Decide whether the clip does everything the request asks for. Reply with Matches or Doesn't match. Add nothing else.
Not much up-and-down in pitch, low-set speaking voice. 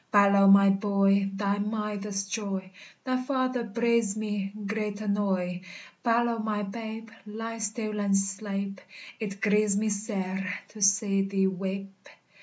Doesn't match